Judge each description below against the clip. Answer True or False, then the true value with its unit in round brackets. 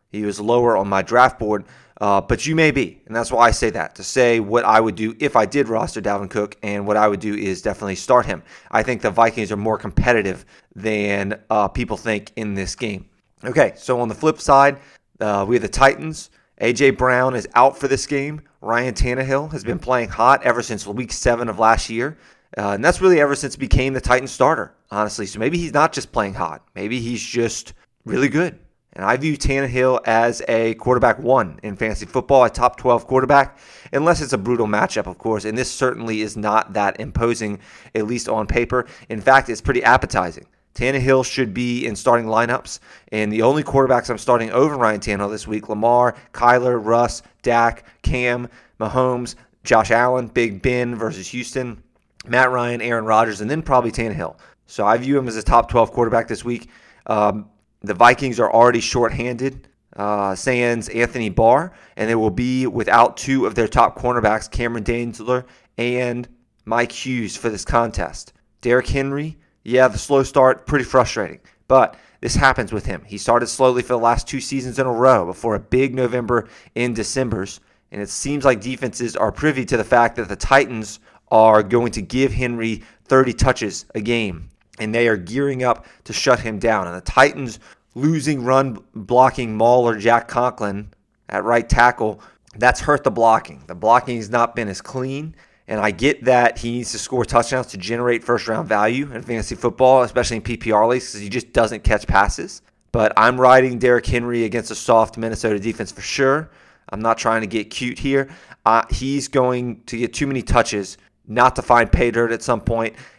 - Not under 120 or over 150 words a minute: False (195 wpm)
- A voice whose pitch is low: True (120 Hz)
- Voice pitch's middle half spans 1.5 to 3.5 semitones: True (2.8 semitones)